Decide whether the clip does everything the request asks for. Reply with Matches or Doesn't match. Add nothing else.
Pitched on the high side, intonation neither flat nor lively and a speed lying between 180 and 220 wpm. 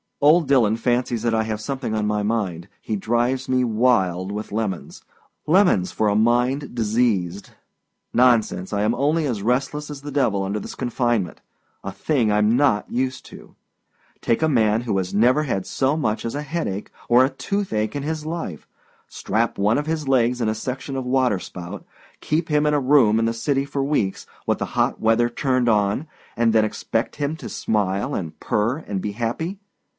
Doesn't match